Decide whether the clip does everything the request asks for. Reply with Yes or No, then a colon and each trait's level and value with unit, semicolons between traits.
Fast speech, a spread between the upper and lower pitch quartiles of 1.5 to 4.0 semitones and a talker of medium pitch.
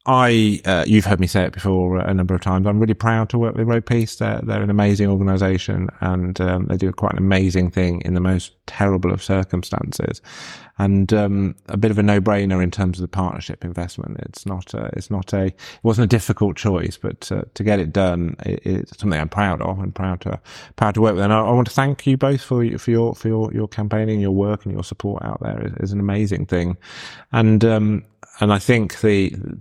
No: fast, 235 wpm; average, 3.0 semitones; low, 100 Hz